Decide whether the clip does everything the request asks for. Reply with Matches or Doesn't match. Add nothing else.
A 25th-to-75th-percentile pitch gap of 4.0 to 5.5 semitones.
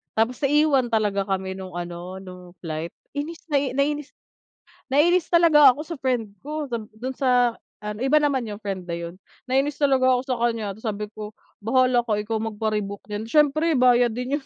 Matches